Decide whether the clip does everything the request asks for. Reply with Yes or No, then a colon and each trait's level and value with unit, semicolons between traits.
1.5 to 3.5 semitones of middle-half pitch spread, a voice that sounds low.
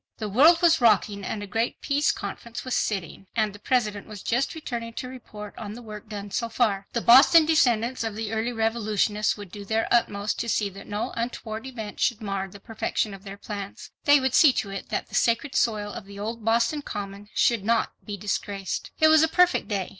No: average, 2.8 semitones; high, 220 Hz